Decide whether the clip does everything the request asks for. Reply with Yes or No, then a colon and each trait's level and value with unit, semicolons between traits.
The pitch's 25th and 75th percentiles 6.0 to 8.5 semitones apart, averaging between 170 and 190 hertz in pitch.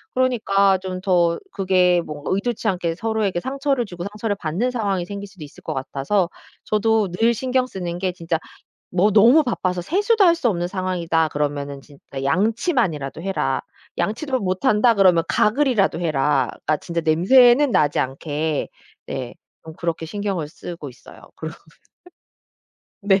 No: average, 5.3 semitones; medium, 185 Hz